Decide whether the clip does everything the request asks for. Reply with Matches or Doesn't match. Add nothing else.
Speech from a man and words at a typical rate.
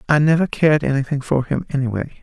Matches